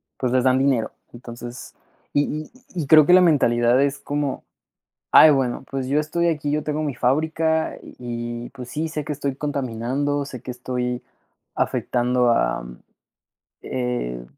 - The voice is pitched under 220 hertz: Yes, low, 135 Hz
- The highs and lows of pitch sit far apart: No, average, 3.3 semitones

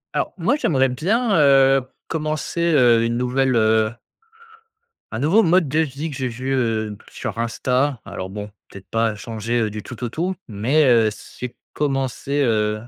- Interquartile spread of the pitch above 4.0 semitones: Yes, average, 4.5 semitones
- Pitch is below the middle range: Yes, low, 125 Hz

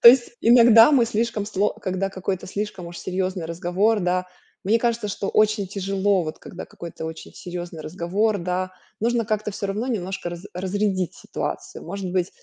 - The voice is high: Yes, high, 195 Hz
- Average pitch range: Yes, average, 3.0 semitones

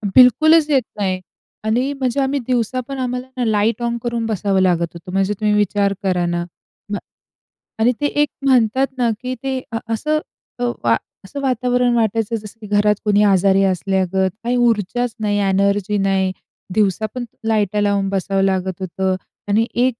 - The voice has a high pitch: Yes, high, 210 Hz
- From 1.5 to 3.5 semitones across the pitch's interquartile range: No, average, 4.1 semitones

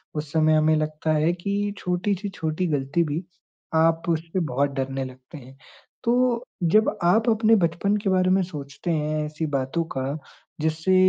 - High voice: No, medium, 160 Hz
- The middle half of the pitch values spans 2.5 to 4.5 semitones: Yes, average, 3.5 semitones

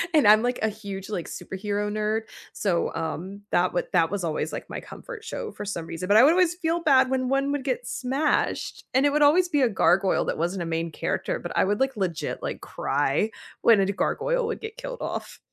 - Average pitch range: No, wide, 7.4 semitones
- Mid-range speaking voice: No, high, 215 Hz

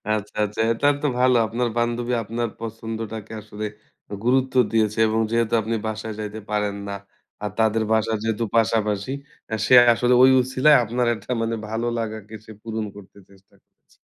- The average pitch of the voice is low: Yes, low, 110 Hz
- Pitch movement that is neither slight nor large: No, narrow, 1.7 semitones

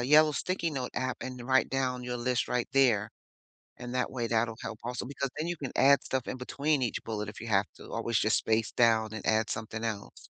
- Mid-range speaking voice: No, low, 125 Hz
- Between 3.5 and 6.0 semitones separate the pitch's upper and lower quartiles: No, average, 3.0 semitones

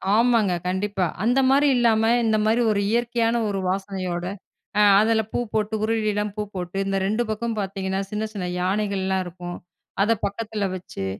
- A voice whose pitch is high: Yes, high, 210 Hz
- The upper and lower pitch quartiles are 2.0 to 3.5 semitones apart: Yes, average, 2.9 semitones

